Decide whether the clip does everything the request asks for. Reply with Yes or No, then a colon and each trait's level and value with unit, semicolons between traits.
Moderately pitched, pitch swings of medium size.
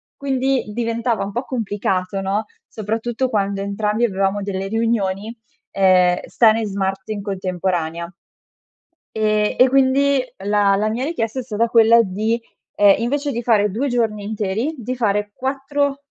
No: high, 215 Hz; average, 3.5 semitones